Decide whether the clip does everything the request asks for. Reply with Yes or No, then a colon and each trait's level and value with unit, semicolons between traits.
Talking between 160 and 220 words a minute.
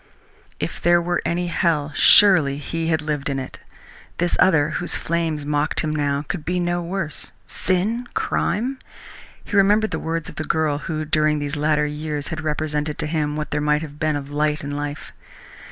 Yes: average, 185 wpm